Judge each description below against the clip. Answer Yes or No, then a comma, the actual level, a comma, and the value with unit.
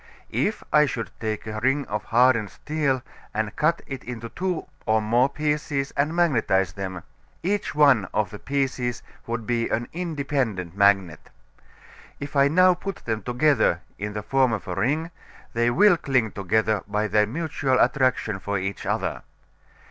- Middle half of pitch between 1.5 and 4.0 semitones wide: No, wide, 5.5 semitones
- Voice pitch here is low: Yes, low, 120 Hz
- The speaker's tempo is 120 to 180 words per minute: Yes, average, 160 wpm